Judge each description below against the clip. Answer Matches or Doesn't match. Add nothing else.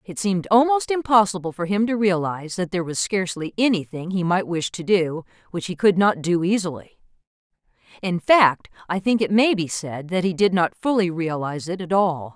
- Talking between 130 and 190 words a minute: Doesn't match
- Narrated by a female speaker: Matches